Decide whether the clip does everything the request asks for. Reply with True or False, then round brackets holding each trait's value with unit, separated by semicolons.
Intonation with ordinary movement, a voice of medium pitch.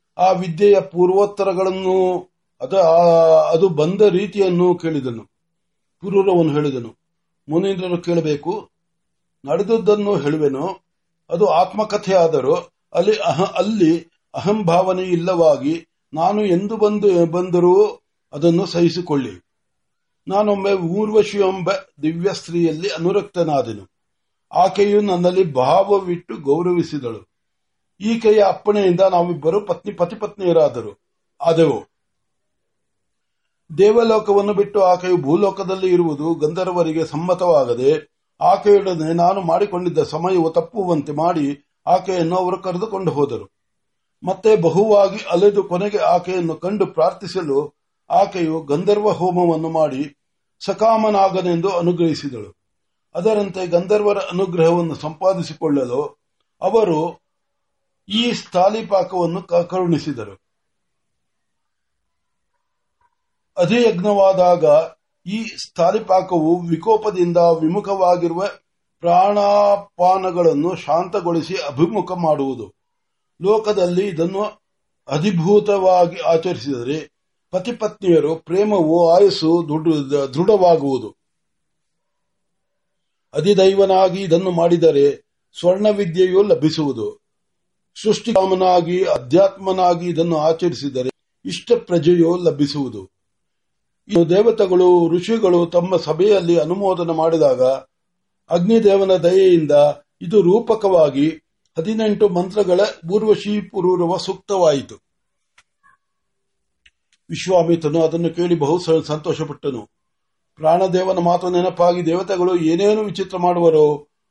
True (3.4 semitones; 180 Hz)